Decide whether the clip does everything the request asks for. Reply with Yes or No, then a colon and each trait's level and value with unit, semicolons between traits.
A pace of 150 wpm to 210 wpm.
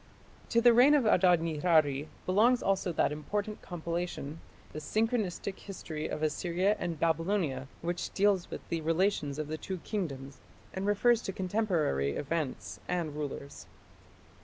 No: average, 140 wpm